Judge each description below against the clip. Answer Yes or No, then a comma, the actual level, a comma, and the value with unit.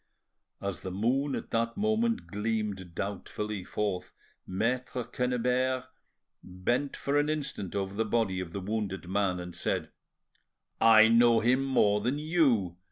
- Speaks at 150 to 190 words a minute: No, average, 140 wpm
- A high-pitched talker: No, low, 110 Hz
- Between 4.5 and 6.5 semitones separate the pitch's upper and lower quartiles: Yes, average, 4.8 semitones